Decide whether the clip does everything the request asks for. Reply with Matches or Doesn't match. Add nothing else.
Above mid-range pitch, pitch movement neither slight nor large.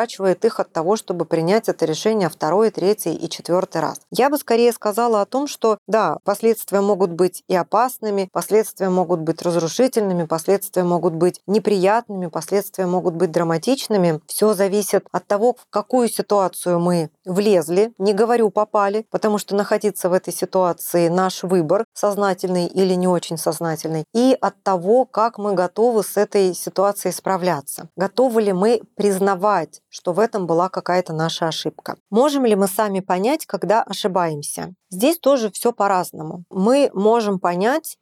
Matches